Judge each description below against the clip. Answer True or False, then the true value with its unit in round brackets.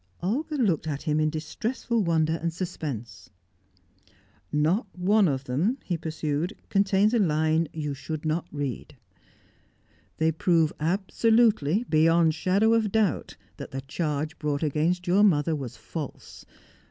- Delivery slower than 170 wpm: True (140 wpm)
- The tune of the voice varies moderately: True (4.5 semitones)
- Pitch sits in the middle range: True (165 Hz)